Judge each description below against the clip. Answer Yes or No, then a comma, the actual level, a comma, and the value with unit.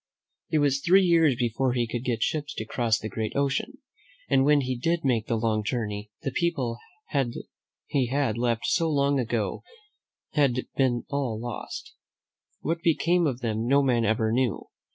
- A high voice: No, low, 125 Hz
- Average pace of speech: Yes, average, 170 wpm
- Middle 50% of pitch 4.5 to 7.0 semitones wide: No, average, 3.7 semitones